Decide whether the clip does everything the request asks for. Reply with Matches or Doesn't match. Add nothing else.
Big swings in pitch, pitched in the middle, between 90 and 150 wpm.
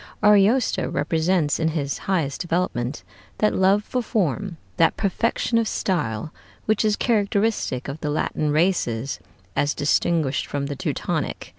Matches